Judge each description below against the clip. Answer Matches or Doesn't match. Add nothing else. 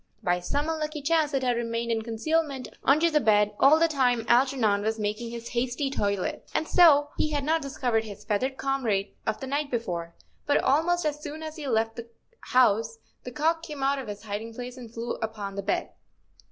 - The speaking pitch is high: Matches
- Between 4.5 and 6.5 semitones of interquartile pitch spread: Matches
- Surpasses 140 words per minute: Matches